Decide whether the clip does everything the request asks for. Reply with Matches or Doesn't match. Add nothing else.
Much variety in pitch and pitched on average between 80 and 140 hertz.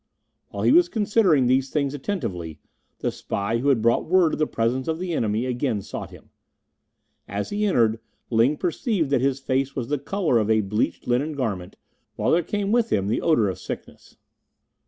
Matches